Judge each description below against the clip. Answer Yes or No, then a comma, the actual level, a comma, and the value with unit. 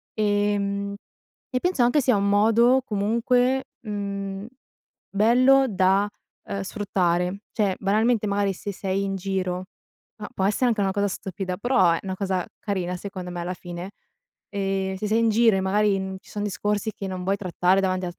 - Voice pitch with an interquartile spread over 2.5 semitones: No, narrow, 2.0 semitones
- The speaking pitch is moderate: No, high, 200 Hz